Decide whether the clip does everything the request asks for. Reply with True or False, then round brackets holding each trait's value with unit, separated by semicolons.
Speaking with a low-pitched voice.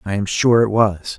True (105 Hz)